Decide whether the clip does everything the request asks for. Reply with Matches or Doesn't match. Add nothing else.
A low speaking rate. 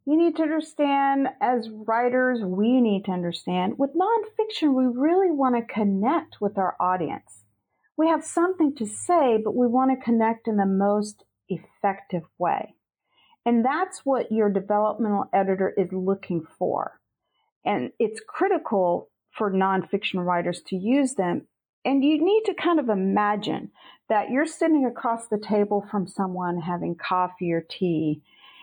Doesn't match